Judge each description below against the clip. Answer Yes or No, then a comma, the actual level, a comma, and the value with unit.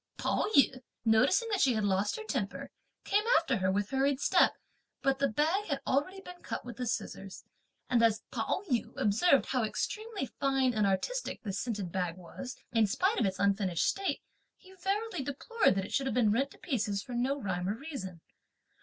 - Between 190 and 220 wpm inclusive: Yes, average, 195 wpm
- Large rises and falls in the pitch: Yes, wide, 6.9 semitones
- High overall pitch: Yes, very high, 250 Hz